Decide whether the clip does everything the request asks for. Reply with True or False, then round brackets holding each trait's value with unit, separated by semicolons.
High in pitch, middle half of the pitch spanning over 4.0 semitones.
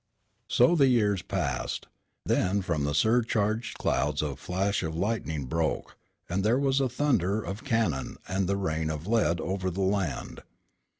False (95 Hz; 5.6 semitones)